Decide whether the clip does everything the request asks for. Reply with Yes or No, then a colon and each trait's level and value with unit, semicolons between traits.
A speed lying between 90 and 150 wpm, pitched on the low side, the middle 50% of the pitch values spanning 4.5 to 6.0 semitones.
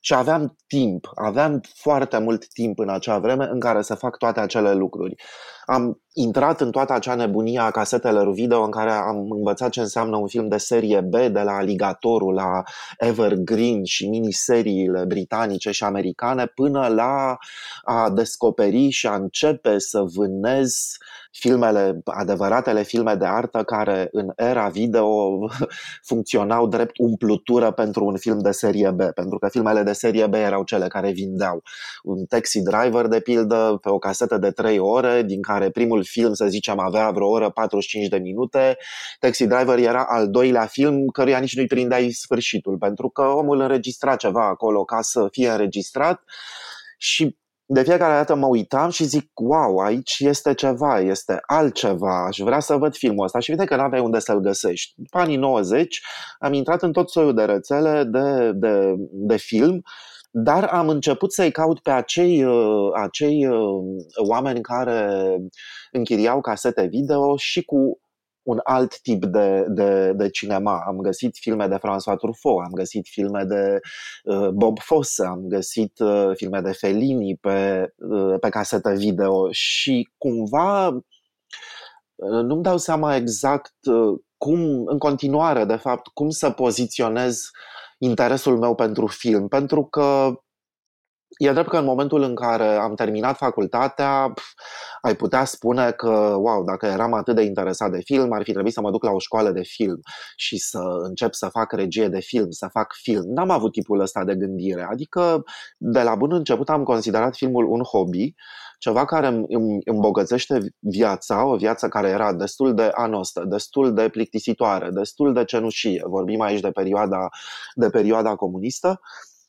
No: average, 160 wpm; low, 115 Hz; average, 4.8 semitones